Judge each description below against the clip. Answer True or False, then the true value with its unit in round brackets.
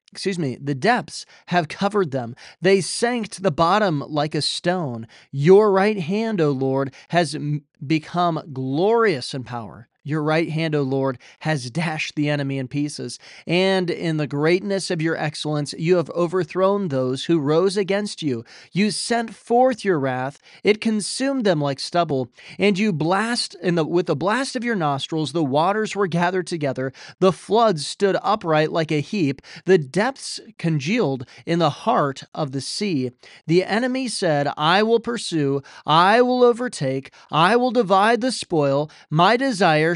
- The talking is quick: False (165 wpm)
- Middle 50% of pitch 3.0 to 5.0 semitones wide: False (5.5 semitones)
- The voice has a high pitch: False (170 Hz)